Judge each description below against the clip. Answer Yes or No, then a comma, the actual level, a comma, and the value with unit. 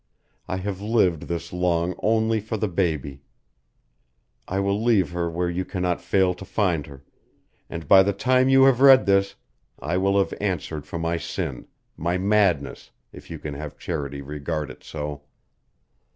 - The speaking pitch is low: Yes, very low, 90 Hz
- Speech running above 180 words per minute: No, average, 165 wpm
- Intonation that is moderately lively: Yes, average, 3.7 semitones